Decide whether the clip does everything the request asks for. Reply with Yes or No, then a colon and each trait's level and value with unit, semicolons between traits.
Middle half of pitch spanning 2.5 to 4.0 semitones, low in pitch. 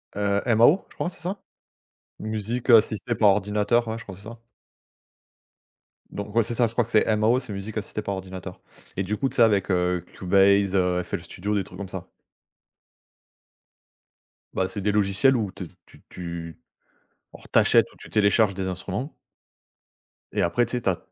Yes: average, 3.2 semitones; low, 100 Hz